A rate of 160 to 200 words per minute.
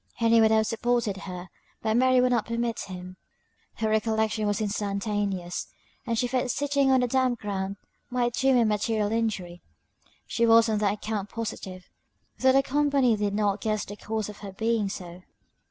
Yes: average, 180 wpm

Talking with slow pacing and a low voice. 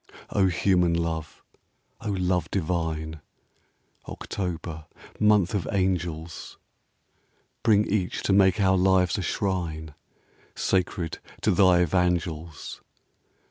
Yes: slow, 100 wpm; very low, 90 Hz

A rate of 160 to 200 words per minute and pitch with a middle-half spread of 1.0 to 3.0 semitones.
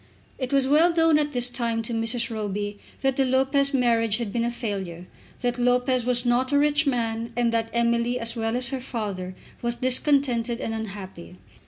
Yes: average, 190 wpm; narrow, 2.6 semitones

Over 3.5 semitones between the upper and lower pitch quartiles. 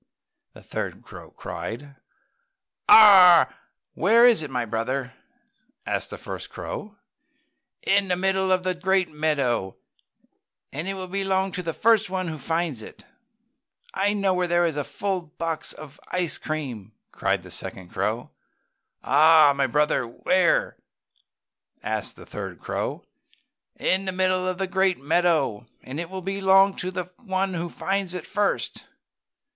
Yes: average, 4.3 semitones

